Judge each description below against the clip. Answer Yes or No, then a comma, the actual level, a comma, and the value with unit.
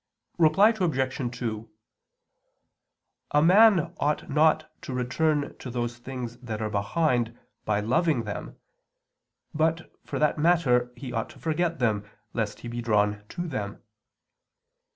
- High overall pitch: No, low, 125 Hz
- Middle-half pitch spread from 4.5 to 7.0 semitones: Yes, wide, 5.5 semitones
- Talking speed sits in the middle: No, slow, 130 wpm